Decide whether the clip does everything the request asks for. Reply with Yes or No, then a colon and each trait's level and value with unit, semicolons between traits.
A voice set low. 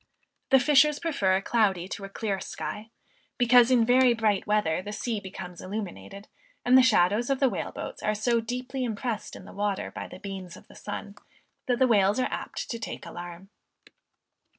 No: high, 215 Hz